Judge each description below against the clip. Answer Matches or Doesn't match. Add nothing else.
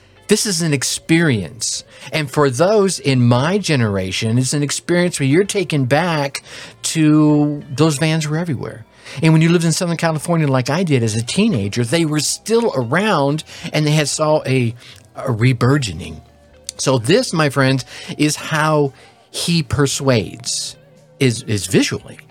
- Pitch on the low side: Doesn't match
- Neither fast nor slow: Matches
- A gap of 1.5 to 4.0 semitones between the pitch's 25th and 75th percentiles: Doesn't match